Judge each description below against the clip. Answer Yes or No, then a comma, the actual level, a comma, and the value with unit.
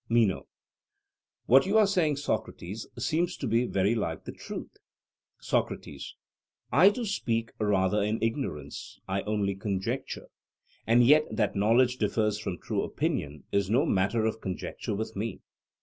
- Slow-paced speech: No, average, 145 wpm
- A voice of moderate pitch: No, low, 110 Hz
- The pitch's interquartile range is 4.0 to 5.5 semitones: Yes, average, 4.6 semitones